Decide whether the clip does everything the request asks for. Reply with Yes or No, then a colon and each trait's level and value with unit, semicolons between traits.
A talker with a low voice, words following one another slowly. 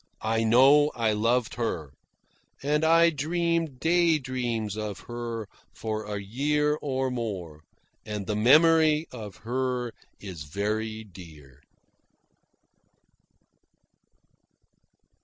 Yes: low, 120 Hz; slow, 100 wpm